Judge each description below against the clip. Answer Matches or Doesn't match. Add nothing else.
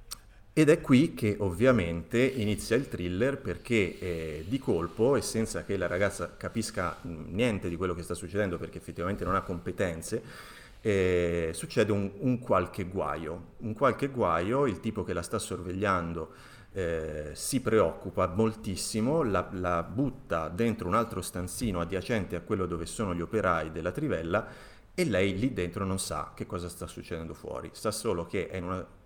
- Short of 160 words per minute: Doesn't match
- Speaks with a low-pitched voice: Matches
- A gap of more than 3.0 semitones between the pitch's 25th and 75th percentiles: Matches